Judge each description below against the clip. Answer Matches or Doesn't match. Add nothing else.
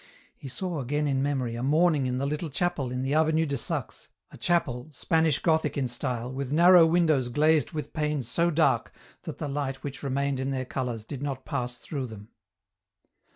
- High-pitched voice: Doesn't match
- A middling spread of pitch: Matches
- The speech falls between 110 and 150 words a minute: Doesn't match